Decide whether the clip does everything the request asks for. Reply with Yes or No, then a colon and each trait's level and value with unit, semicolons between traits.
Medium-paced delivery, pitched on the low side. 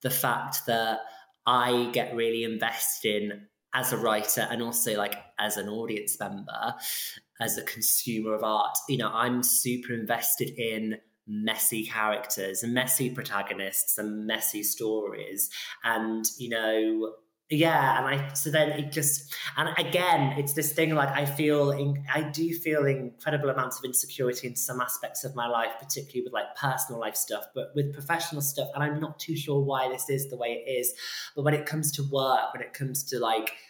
Yes: average, 180 wpm; low, 125 Hz